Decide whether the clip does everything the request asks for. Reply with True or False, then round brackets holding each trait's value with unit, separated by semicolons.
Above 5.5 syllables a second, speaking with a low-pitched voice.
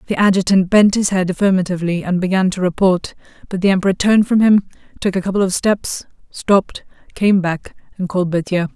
False (6.0 syllables/s; 190 Hz)